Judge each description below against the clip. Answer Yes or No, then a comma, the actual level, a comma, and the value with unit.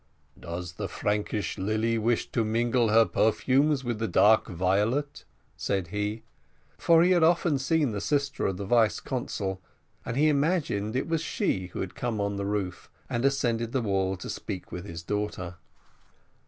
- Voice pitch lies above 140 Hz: No, low, 110 Hz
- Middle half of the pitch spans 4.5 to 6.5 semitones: Yes, average, 5.2 semitones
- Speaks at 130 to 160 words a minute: No, average, 170 wpm